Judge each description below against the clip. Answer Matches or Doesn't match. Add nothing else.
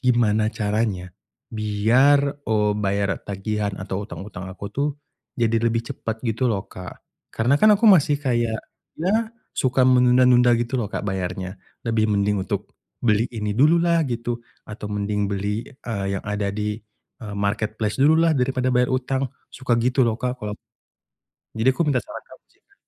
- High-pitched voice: Doesn't match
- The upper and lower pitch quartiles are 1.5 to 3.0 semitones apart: Doesn't match